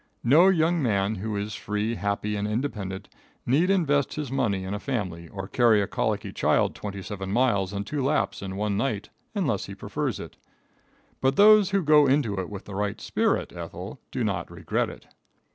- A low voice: Yes, low, 105 Hz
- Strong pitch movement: Yes, wide, 5.7 semitones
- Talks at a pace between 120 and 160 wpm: No, average, 190 wpm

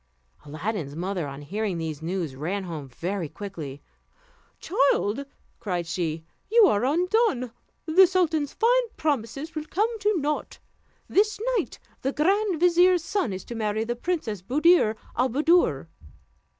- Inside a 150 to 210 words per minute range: No, slow, 135 wpm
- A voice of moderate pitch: No, high, 240 Hz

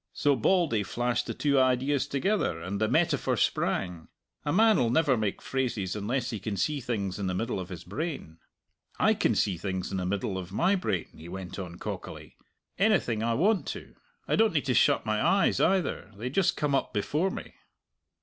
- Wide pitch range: Yes, wide, 7.5 semitones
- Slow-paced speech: No, average, 195 wpm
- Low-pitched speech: Yes, low, 120 Hz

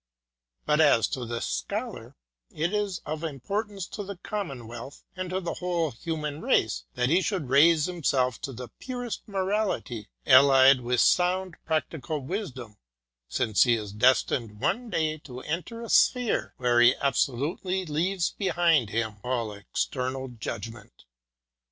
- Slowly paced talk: No, average, 145 wpm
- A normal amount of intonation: No, wide, 6.7 semitones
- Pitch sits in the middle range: Yes, medium, 150 Hz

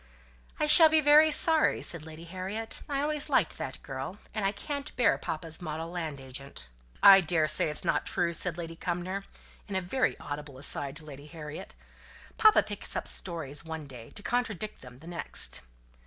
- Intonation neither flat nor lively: No, wide, 6.0 semitones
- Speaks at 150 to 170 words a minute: No, average, 180 wpm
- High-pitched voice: No, medium, 170 Hz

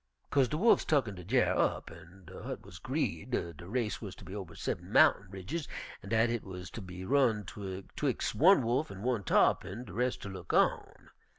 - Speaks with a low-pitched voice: Yes, low, 105 Hz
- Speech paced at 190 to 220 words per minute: Yes, average, 200 wpm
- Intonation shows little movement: No, average, 5.1 semitones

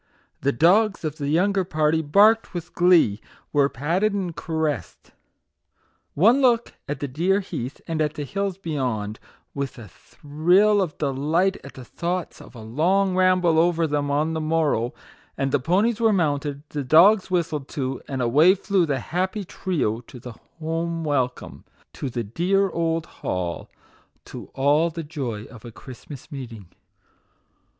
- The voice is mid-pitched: Yes, medium, 155 Hz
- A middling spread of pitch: Yes, average, 5.0 semitones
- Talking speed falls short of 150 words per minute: No, average, 160 wpm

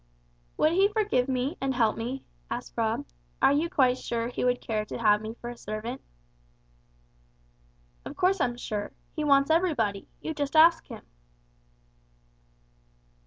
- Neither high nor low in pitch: No, very high, 255 Hz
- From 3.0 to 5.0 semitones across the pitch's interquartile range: No, wide, 5.4 semitones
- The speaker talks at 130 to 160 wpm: Yes, average, 150 wpm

